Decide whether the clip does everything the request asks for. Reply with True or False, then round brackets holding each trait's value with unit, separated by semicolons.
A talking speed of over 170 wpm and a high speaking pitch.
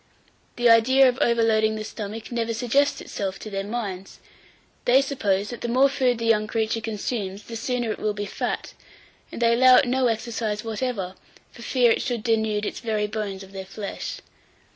True (185 wpm; 225 Hz)